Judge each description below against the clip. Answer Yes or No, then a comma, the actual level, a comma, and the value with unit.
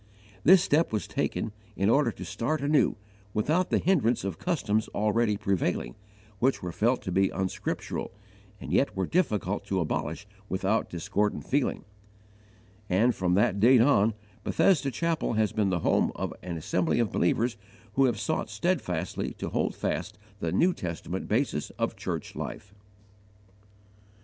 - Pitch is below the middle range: Yes, low, 105 Hz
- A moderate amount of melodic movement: No, wide, 6.2 semitones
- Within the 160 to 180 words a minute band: No, average, 150 wpm